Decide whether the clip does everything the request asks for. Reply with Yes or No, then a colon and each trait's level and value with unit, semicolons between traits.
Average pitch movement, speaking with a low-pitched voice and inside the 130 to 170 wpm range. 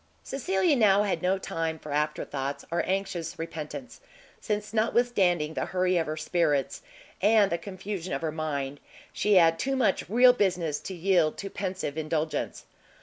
No: average, 4.2 semitones; medium, 180 Hz; average, 155 wpm